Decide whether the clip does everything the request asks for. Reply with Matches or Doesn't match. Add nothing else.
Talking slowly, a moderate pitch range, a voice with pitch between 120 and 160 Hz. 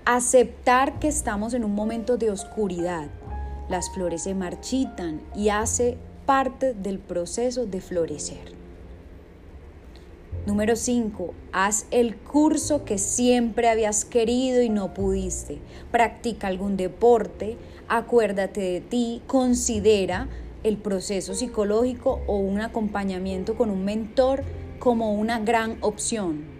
Doesn't match